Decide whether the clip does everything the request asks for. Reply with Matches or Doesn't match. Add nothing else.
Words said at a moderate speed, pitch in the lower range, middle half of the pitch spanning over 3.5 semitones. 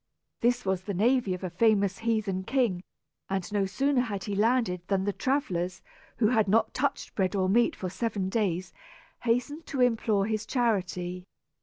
Doesn't match